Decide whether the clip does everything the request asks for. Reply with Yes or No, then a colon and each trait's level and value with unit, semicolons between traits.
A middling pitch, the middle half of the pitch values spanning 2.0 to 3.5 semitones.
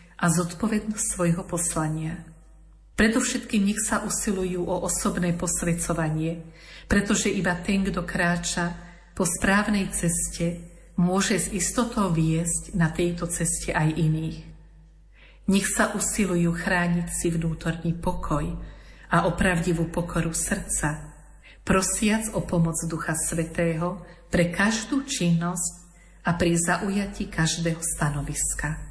Yes: medium, 175 Hz; average, 2.8 semitones